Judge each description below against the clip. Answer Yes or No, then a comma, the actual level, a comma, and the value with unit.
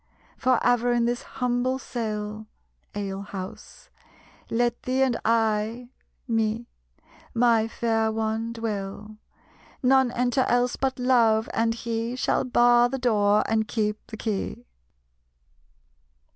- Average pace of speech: No, slow, 115 wpm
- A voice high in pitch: Yes, high, 230 Hz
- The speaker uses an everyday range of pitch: No, narrow, 2.0 semitones